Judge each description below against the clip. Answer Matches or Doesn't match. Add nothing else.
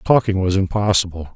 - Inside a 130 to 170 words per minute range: Matches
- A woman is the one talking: Doesn't match